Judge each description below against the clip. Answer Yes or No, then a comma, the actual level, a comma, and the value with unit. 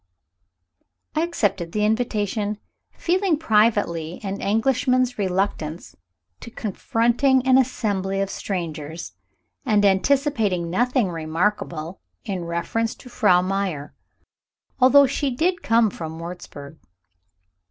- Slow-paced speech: Yes, slow, 100 wpm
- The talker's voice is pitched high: Yes, high, 205 Hz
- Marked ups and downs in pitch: Yes, wide, 5.9 semitones